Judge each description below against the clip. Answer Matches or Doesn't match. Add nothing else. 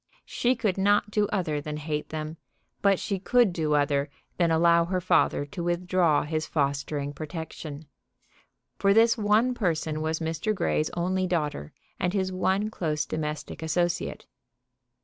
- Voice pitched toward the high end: Doesn't match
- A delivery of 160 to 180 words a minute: Doesn't match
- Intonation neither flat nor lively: Matches